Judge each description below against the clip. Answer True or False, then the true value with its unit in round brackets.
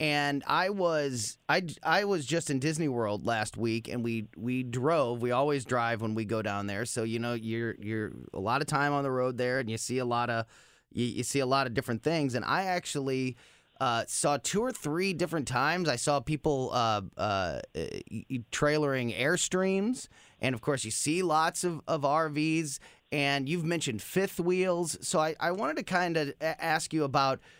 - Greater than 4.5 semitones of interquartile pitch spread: True (5.2 semitones)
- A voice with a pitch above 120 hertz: True (140 Hz)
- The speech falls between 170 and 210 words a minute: True (200 wpm)